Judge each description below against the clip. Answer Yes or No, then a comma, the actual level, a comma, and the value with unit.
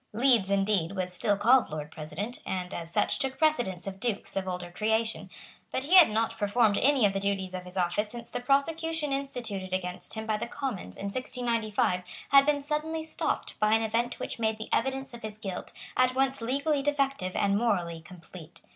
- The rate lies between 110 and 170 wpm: No, average, 195 wpm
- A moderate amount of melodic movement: No, wide, 5.8 semitones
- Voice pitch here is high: Yes, high, 220 Hz